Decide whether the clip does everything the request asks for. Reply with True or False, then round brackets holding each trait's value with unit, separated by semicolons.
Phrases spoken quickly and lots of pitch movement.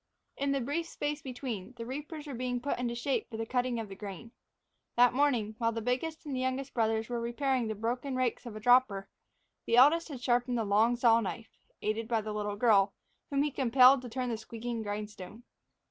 False (210 wpm; 2.8 semitones)